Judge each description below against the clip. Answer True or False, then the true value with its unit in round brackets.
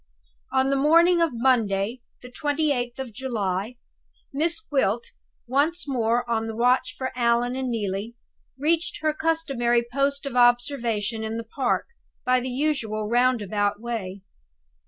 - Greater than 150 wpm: False (135 wpm)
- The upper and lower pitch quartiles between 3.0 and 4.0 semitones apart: True (3.6 semitones)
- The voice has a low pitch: False (245 Hz)